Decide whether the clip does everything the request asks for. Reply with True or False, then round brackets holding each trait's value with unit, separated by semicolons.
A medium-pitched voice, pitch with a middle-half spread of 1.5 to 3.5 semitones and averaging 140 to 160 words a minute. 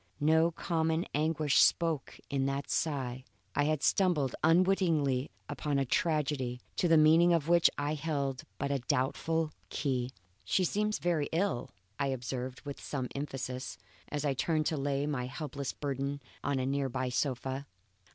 True (145 Hz; 3.1 semitones; 155 wpm)